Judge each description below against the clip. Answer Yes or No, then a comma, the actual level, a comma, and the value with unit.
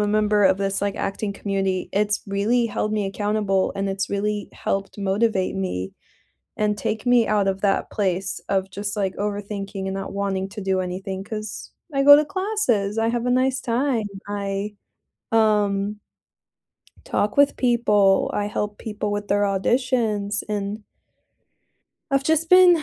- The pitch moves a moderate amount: No, narrow, 2.2 semitones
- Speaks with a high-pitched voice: Yes, high, 205 Hz